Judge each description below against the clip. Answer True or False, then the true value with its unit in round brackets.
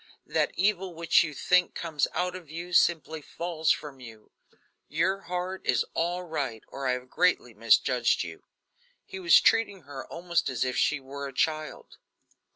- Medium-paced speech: True (165 wpm)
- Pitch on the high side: False (160 Hz)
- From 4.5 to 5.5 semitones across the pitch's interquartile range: True (5.0 semitones)